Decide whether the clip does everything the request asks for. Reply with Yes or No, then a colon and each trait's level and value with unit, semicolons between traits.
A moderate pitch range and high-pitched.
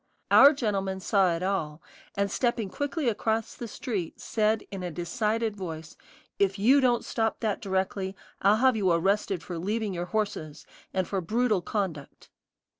Yes: average, 3.2 semitones; high, 200 Hz